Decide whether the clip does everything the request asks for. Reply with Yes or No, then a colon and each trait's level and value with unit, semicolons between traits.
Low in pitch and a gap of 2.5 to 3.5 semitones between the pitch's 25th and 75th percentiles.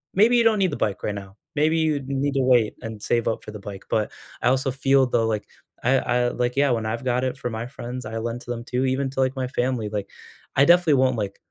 Yes: low, 125 Hz; average, 3.2 semitones